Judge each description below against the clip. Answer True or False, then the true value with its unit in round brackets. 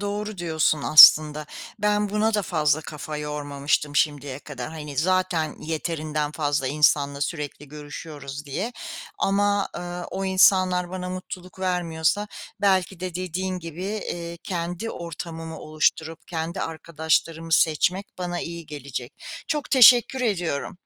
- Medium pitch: True (165 Hz)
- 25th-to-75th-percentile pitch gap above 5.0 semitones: False (3.6 semitones)